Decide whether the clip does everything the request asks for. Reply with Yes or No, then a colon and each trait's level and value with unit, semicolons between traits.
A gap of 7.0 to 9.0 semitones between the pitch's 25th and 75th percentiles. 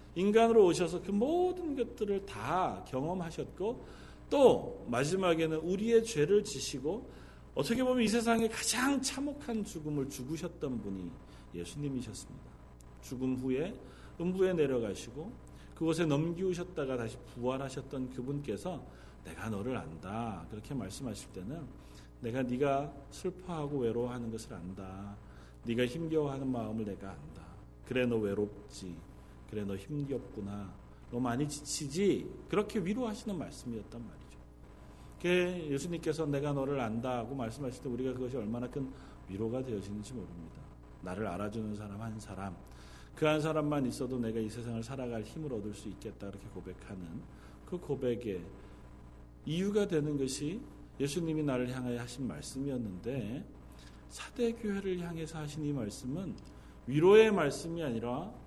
Yes: wide, 7.9 semitones